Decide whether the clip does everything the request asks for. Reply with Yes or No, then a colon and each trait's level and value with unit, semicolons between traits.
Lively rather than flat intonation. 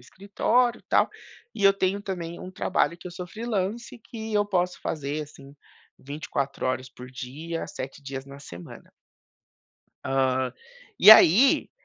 Yes: wide, 6.6 semitones